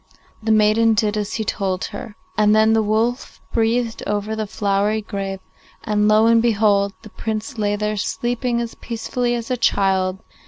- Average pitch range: No, narrow, 1.8 semitones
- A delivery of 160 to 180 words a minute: Yes, average, 170 wpm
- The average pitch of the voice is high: Yes, high, 215 Hz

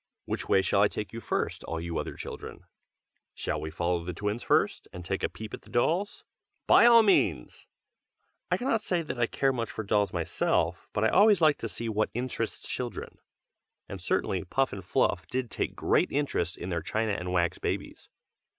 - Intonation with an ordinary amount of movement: No, wide, 6.8 semitones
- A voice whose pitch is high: No, low, 110 Hz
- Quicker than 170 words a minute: Yes, average, 195 wpm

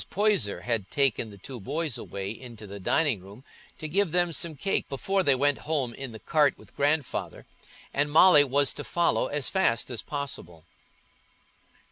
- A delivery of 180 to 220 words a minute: No, average, 170 wpm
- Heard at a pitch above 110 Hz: Yes, medium, 140 Hz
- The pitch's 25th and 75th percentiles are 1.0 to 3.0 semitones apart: No, wide, 5.5 semitones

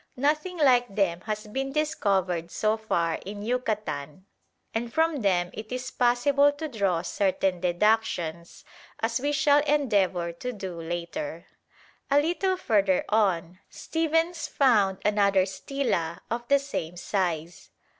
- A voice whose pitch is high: Yes, high, 215 Hz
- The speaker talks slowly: Yes, slow, 130 wpm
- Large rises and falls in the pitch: Yes, wide, 7.4 semitones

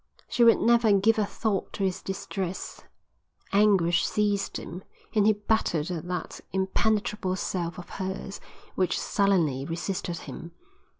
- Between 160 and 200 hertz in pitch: Yes, high, 190 Hz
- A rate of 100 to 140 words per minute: Yes, slow, 135 wpm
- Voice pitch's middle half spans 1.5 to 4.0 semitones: Yes, average, 2.9 semitones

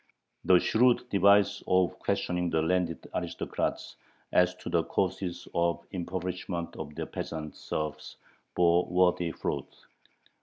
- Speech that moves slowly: Yes, slow, 125 wpm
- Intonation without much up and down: Yes, narrow, 1.5 semitones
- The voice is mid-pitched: No, very low, 90 Hz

